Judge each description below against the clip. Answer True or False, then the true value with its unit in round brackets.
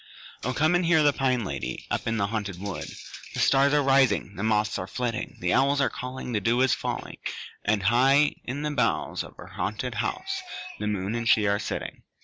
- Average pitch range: True (4.8 semitones)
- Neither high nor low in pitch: False (120 Hz)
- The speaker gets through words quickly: True (210 wpm)